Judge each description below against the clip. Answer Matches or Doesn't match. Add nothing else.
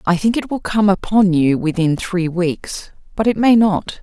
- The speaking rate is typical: Doesn't match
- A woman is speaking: Matches